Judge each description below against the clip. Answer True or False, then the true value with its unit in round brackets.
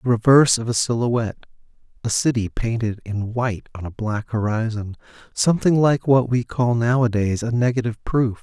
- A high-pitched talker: False (115 Hz)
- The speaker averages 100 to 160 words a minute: True (155 wpm)